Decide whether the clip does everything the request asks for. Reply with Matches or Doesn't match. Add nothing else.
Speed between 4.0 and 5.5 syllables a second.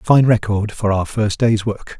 Matches